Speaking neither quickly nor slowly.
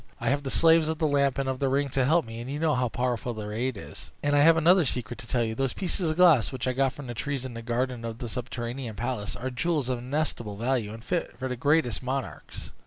No: fast, 270 wpm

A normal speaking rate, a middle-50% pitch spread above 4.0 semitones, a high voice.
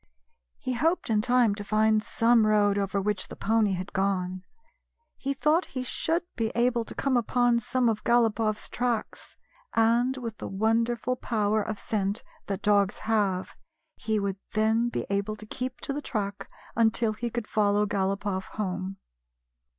No: average, 160 wpm; average, 2.8 semitones; high, 215 Hz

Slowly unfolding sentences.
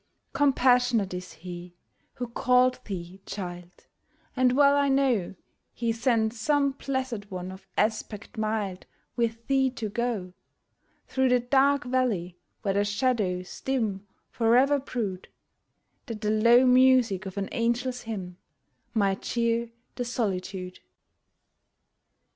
Yes: slow, 120 wpm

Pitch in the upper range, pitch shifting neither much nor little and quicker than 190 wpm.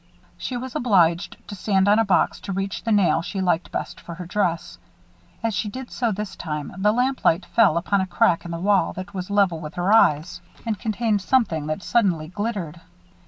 Yes: high, 195 Hz; average, 3.8 semitones; fast, 205 wpm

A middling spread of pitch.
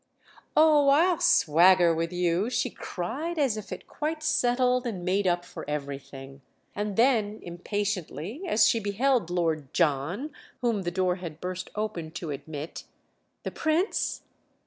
No: wide, 6.5 semitones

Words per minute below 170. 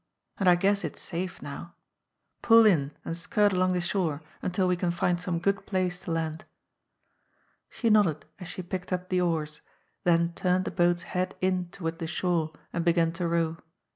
No: average, 185 wpm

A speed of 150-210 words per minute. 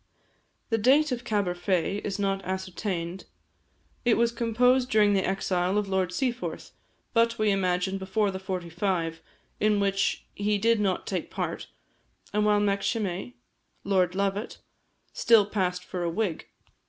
No: average, 140 wpm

